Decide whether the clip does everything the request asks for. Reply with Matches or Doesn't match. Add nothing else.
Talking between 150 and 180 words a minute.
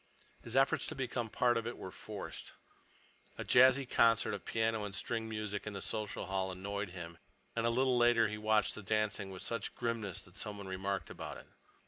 Doesn't match